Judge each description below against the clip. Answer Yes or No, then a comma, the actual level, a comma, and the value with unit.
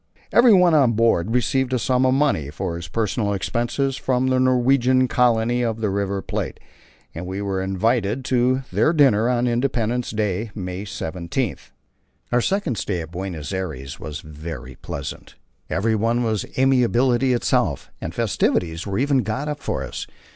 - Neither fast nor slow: Yes, average, 155 wpm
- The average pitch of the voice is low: Yes, low, 115 Hz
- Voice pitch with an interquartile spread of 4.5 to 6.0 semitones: Yes, average, 5.2 semitones